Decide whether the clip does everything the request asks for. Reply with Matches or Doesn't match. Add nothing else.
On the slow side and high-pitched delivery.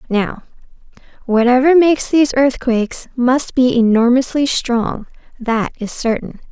Matches